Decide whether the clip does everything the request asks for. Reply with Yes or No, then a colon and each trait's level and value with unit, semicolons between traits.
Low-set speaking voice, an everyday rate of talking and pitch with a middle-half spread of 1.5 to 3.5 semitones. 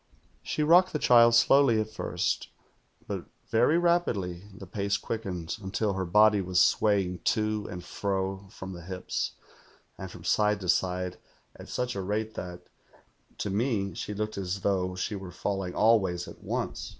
Yes: low, 100 Hz; average, 165 wpm; average, 3.0 semitones